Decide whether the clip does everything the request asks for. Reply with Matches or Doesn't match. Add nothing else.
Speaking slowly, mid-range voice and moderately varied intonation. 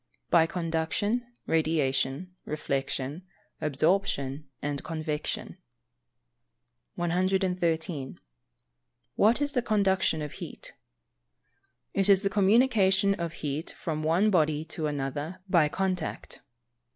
Matches